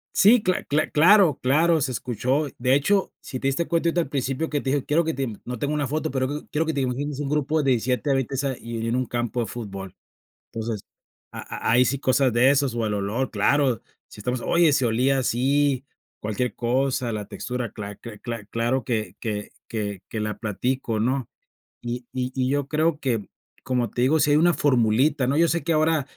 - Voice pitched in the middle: No, low, 130 Hz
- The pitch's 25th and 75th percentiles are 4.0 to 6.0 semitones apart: No, average, 3.6 semitones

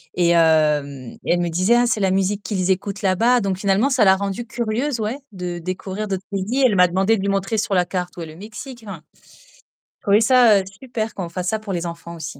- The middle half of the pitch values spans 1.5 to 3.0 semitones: No, average, 3.4 semitones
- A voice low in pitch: No, high, 195 Hz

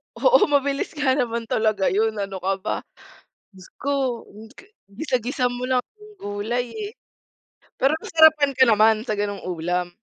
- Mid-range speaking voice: No, high, 240 Hz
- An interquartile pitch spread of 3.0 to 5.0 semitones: No, wide, 5.6 semitones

